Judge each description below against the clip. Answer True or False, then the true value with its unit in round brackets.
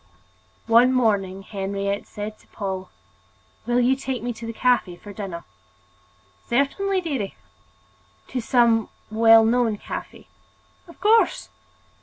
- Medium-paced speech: False (120 wpm)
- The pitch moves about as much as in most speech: True (3.8 semitones)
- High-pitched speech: True (225 Hz)